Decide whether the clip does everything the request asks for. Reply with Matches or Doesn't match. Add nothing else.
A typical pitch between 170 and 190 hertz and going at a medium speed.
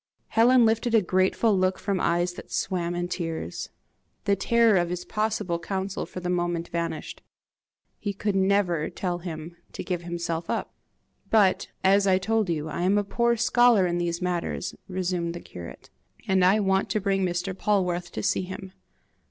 Matches